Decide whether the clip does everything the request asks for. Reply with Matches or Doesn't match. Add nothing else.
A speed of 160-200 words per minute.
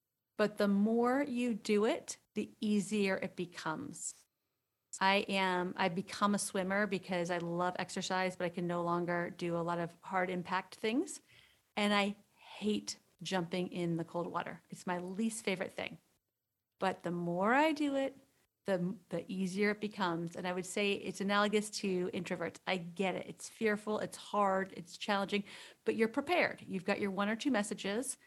Matches